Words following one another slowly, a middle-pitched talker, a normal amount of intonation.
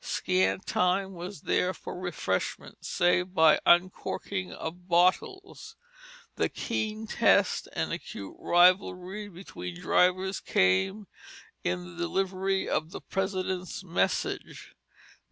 Yes: slow, 105 wpm; medium, 180 Hz; average, 3.0 semitones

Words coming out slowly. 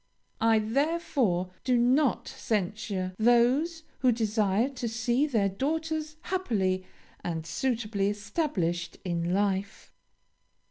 Yes: slow, 100 wpm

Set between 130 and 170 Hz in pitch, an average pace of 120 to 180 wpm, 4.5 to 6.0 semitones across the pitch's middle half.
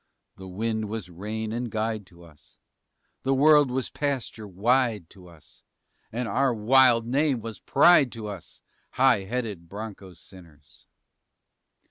No: low, 110 Hz; slow, 135 wpm; average, 4.9 semitones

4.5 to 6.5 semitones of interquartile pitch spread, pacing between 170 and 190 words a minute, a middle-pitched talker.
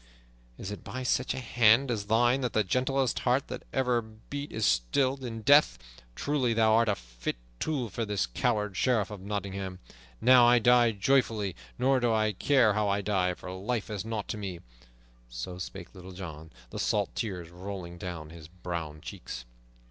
No: average, 4.9 semitones; average, 180 wpm; low, 105 Hz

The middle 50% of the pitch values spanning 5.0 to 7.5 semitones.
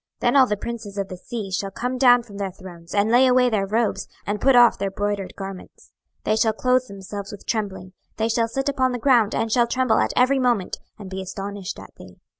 No: average, 3.8 semitones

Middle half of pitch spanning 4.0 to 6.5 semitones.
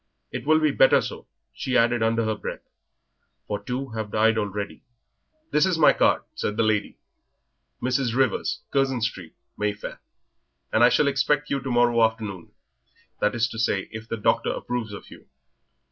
No: average, 3.5 semitones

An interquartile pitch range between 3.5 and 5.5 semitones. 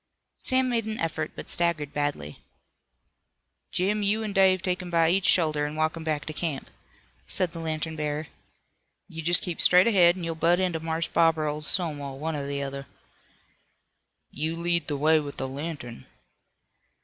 No: average, 3.1 semitones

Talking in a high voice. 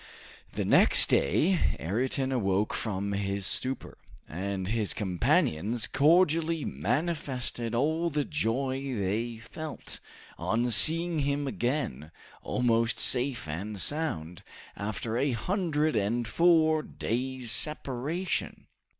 No: low, 125 Hz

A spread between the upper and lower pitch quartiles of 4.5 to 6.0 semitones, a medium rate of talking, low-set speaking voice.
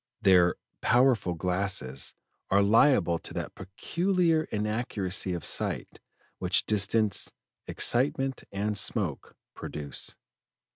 No: average, 5.1 semitones; slow, 95 wpm; low, 100 Hz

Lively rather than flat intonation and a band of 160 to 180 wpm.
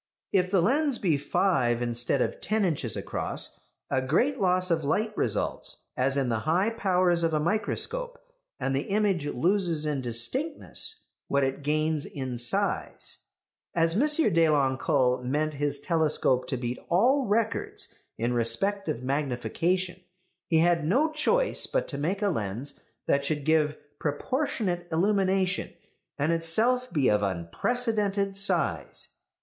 No: wide, 6.7 semitones; average, 140 wpm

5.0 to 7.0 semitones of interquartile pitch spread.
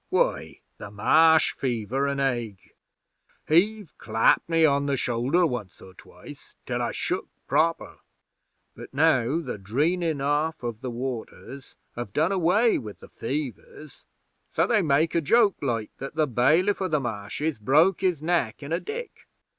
Yes: wide, 5.4 semitones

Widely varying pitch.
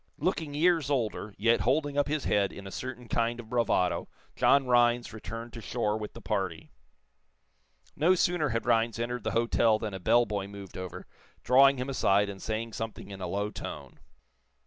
No: average, 3.9 semitones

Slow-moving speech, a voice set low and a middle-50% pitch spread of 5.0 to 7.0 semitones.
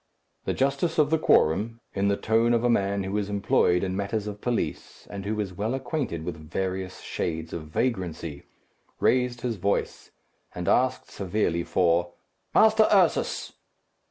No: average, 155 wpm; low, 100 Hz; average, 5.3 semitones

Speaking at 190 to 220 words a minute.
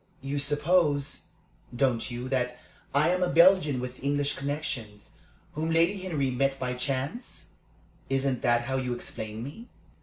No: average, 145 wpm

